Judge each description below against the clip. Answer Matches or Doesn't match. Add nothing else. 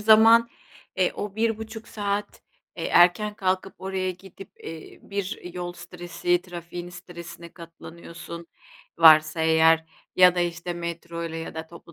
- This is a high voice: Doesn't match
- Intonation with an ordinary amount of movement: Doesn't match